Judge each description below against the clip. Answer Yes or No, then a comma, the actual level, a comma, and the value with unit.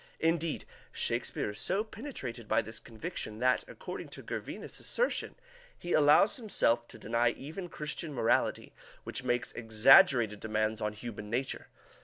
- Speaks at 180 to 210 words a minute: No, average, 140 wpm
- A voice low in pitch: Yes, low, 120 Hz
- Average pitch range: No, wide, 6.6 semitones